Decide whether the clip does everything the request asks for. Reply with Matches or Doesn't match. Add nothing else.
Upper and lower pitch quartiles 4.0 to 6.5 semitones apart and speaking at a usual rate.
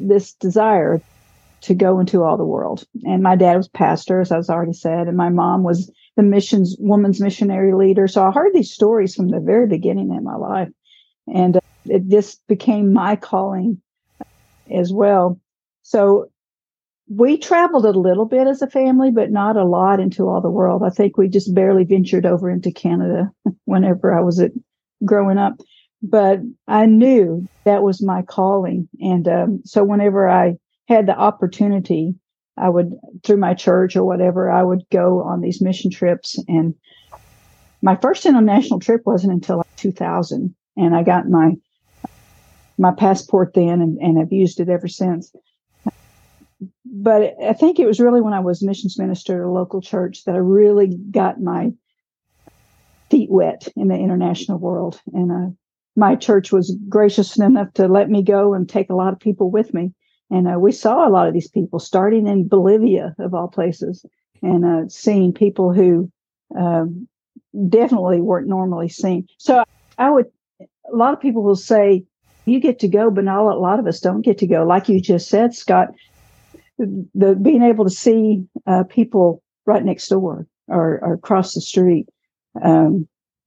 Doesn't match